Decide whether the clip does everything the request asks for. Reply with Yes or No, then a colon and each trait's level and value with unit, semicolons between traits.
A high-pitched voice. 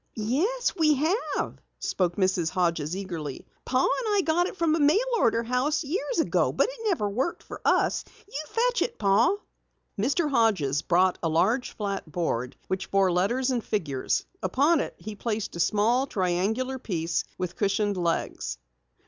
Yes: high, 215 Hz